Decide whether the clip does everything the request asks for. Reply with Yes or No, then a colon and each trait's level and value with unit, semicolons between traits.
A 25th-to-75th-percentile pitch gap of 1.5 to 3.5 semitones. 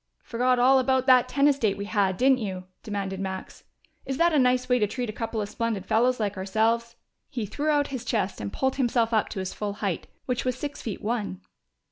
No: average, 4.0 semitones